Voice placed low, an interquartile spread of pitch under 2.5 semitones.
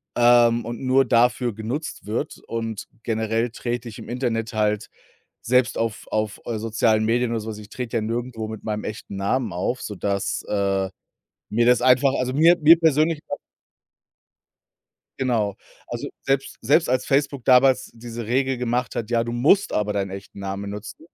No: low, 115 Hz; average, 2.8 semitones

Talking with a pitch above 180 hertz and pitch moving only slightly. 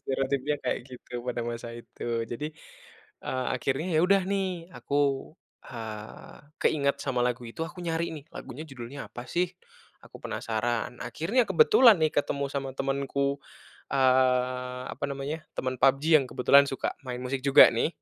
No: low, 135 Hz; narrow, 2.3 semitones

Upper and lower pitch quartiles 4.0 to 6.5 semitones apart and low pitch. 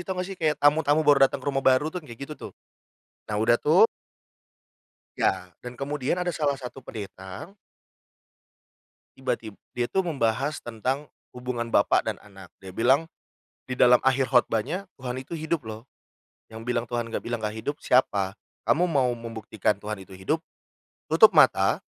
Yes: average, 4.7 semitones; low, 125 Hz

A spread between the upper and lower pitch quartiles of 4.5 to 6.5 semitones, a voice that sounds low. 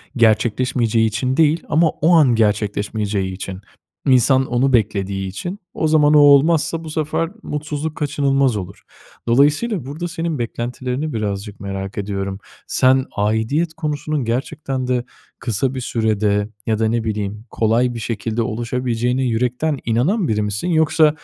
Yes: wide, 5.5 semitones; low, 125 Hz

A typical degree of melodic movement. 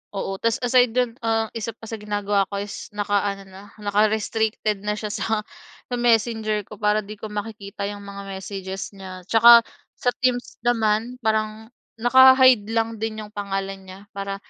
No: narrow, 2.1 semitones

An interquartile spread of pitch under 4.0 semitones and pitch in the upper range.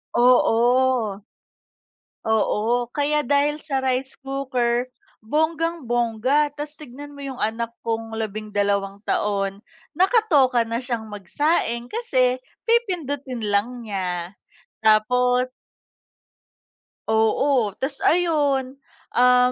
No: average, 4.4 semitones; very high, 250 Hz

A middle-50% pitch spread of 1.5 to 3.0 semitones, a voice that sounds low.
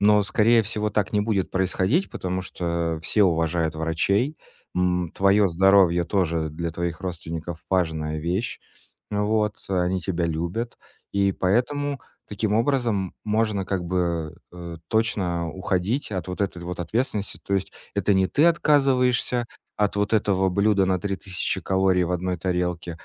No: average, 3.4 semitones; very low, 95 Hz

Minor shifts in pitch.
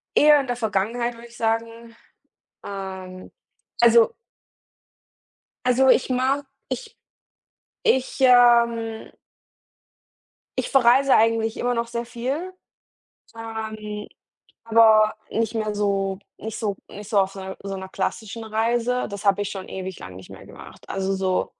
No: average, 3.1 semitones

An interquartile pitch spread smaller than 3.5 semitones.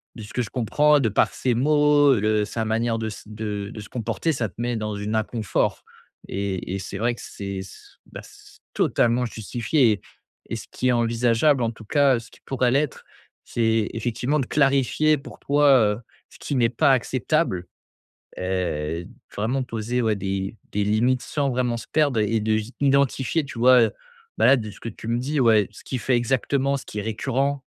No: average, 3.8 semitones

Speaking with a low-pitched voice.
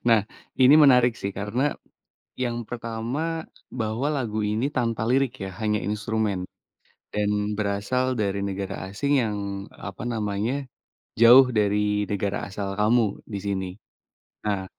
Yes: low, 110 Hz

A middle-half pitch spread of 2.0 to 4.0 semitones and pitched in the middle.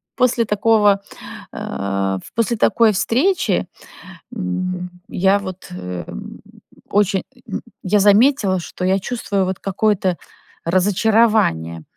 No: average, 3.3 semitones; high, 195 Hz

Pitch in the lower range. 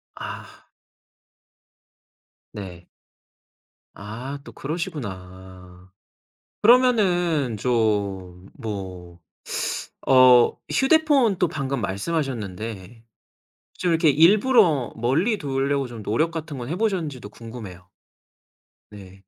Yes: low, 125 Hz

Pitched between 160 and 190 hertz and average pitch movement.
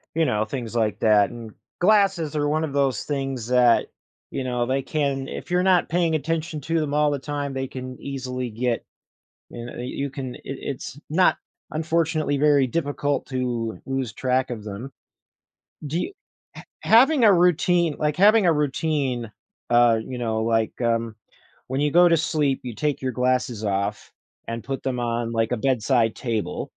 No: low, 135 Hz; average, 4.3 semitones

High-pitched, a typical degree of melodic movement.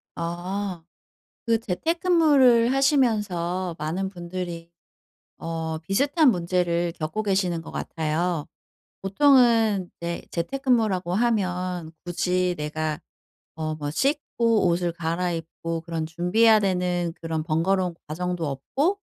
No: medium, 180 Hz; average, 4.7 semitones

